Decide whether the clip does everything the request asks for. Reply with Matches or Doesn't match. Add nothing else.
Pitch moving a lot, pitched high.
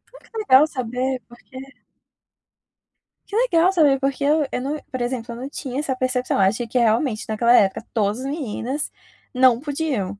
Doesn't match